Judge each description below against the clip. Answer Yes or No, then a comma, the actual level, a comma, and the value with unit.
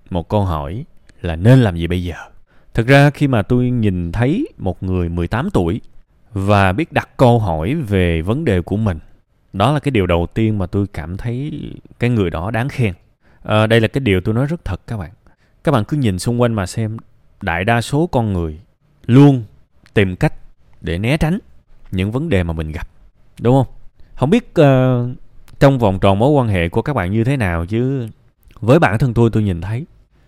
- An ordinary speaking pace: Yes, average, 210 wpm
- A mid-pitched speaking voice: No, low, 110 Hz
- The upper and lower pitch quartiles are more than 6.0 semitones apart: No, wide, 5.6 semitones